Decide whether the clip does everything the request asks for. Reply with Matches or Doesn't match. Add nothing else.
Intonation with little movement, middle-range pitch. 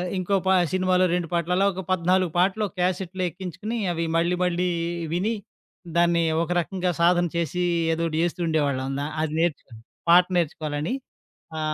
Matches